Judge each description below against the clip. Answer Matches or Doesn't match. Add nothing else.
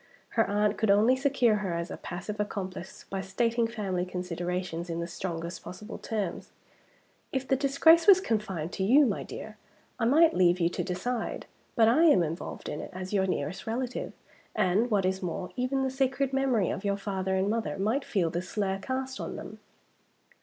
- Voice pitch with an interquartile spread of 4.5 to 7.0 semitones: Matches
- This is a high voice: Matches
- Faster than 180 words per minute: Matches